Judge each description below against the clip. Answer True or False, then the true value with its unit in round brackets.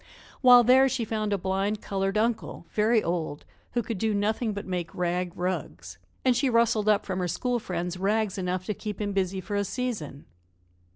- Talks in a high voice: True (205 Hz)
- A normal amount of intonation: True (3.6 semitones)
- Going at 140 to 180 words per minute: False (190 wpm)